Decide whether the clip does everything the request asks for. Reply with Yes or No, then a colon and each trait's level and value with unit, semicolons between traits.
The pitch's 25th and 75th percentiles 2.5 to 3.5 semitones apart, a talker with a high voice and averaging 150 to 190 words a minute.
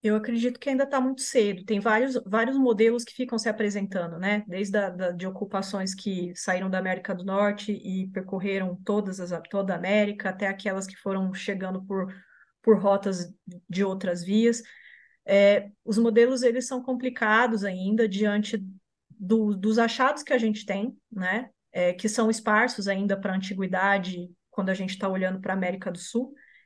Yes: average, 3.0 semitones; high, 200 Hz; average, 180 wpm